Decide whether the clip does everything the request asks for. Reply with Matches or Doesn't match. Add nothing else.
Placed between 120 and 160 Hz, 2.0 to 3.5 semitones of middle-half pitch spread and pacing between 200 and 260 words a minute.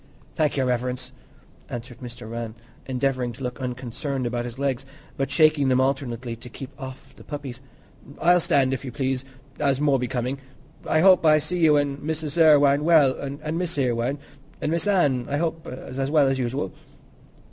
Doesn't match